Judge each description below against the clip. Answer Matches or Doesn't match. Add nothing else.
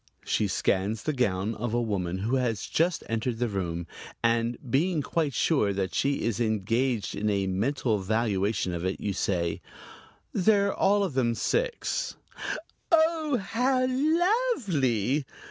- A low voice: Matches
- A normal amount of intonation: Doesn't match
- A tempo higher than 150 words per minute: Doesn't match